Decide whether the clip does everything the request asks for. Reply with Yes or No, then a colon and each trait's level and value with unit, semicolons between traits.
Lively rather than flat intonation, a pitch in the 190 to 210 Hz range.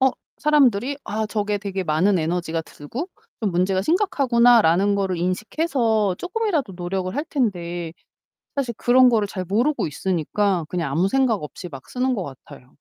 Yes: wide, 6.0 semitones; high, 200 Hz